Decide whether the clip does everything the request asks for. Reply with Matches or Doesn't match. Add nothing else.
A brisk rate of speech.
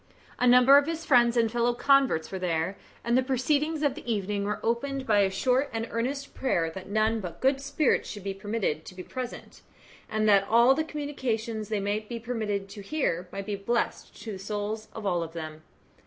Matches